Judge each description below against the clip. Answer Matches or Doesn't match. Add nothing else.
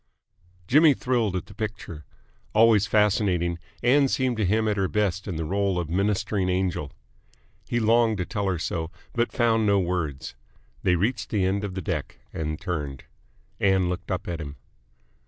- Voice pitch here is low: Matches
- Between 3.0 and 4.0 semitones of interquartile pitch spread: Matches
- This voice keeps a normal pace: Matches